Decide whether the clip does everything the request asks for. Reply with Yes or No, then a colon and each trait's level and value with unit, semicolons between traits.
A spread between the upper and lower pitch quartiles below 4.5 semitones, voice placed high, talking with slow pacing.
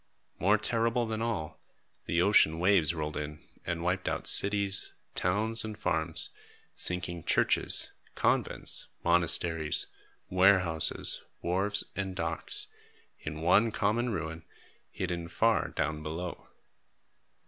No: average, 4.0 semitones; very low, 90 Hz; slow, 110 wpm